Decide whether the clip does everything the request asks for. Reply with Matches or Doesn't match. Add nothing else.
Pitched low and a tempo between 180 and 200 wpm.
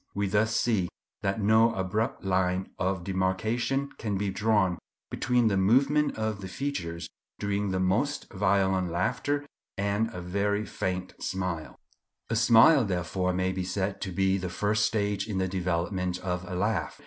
Doesn't match